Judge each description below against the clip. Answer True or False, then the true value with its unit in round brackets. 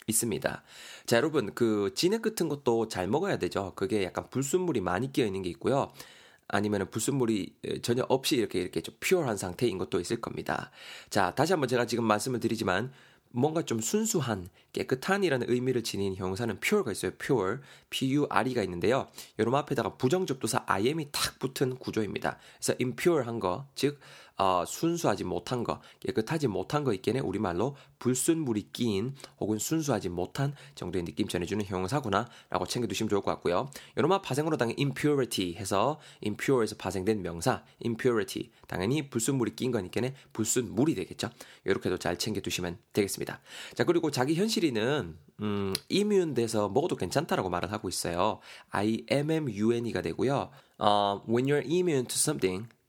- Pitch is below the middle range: True (120 Hz)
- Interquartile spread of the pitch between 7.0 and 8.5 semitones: False (5.4 semitones)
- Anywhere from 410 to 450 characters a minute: True (420 characters per minute)